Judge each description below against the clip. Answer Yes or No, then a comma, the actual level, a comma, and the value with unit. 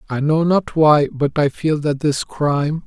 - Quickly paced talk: Yes, fast, 210 wpm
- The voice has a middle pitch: Yes, medium, 150 Hz